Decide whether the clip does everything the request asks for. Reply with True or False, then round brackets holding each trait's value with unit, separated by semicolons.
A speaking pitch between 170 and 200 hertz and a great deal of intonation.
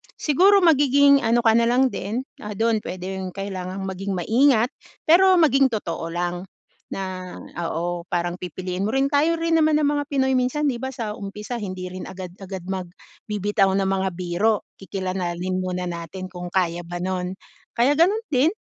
True (195 Hz; 6.3 semitones)